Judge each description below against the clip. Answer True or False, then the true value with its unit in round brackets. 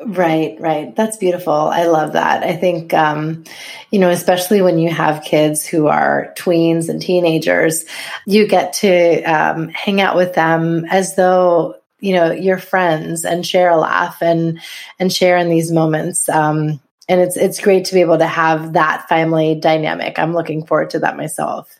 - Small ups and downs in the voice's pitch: True (2.2 semitones)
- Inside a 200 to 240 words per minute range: False (180 wpm)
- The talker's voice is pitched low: False (170 Hz)